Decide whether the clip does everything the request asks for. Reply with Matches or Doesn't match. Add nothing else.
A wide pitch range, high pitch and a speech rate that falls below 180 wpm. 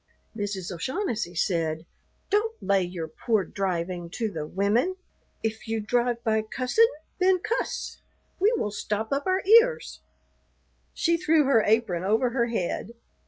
Matches